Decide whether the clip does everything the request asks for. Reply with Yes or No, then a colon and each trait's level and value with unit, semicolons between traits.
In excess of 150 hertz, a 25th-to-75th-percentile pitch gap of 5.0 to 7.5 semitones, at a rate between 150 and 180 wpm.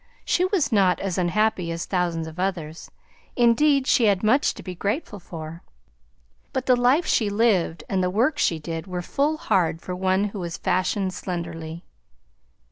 Yes: high, 190 Hz; average, 5.3 semitones; average, 170 wpm